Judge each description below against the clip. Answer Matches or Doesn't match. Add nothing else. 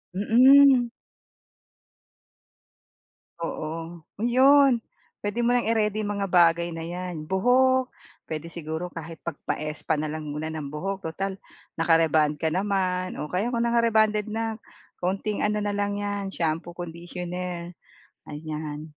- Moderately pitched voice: Matches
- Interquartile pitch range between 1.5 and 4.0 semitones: Doesn't match